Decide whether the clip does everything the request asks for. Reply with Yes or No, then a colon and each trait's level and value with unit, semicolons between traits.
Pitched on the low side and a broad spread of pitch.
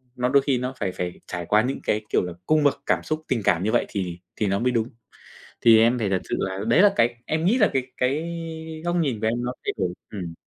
Yes: low, 120 Hz; wide, 5.7 semitones